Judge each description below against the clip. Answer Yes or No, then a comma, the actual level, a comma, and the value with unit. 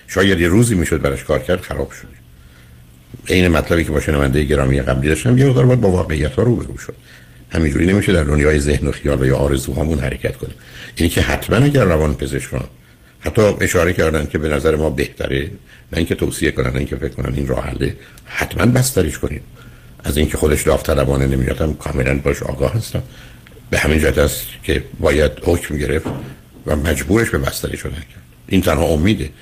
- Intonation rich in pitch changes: No, average, 4.2 semitones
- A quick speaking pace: Yes, fast, 180 wpm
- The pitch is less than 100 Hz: Yes, very low, 75 Hz